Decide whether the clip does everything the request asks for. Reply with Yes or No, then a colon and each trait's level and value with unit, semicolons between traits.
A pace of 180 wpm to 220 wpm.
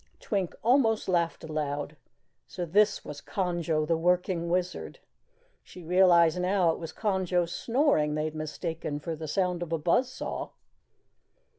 No: average, 145 wpm